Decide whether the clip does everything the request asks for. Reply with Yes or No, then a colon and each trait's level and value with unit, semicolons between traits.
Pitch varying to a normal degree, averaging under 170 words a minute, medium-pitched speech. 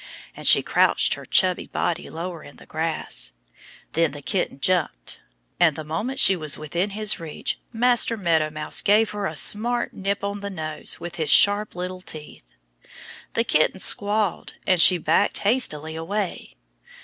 Yes: average, 4.6 semitones; average, 160 wpm; medium, 180 Hz